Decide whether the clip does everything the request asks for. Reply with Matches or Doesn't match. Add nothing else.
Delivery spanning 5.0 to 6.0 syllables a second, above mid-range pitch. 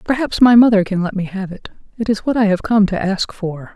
Matches